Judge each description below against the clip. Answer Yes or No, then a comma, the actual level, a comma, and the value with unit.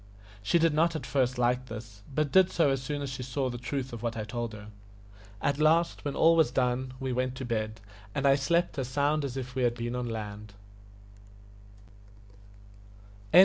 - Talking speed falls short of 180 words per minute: No, average, 190 wpm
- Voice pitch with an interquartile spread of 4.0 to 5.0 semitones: No, average, 3.3 semitones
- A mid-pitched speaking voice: No, low, 130 Hz